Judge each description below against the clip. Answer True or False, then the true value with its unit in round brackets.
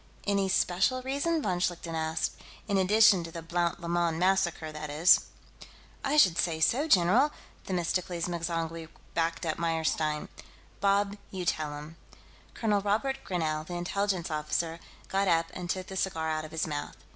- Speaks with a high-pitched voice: False (175 Hz)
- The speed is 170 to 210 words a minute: False (155 wpm)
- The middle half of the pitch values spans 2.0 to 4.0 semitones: True (3.3 semitones)